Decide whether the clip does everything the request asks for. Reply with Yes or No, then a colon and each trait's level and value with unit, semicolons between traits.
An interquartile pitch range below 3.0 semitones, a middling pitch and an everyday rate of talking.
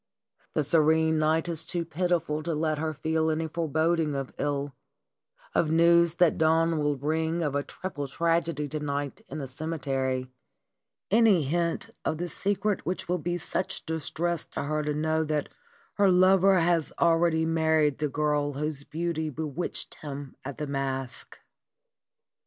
Yes: narrow, 2.4 semitones; medium, 160 Hz; average, 160 wpm